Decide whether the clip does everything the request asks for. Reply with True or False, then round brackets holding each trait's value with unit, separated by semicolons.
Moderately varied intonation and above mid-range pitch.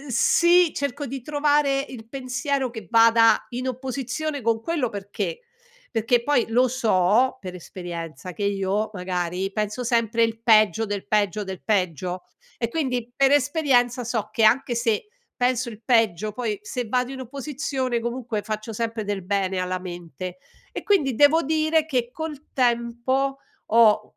True (4.2 semitones; 235 Hz)